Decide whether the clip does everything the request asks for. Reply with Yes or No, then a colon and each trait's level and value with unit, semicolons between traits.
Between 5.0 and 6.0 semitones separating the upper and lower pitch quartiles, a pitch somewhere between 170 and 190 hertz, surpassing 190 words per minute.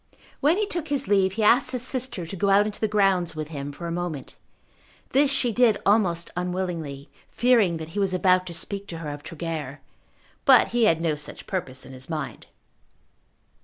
Yes: wide, 5.4 semitones; medium, 185 Hz; average, 200 wpm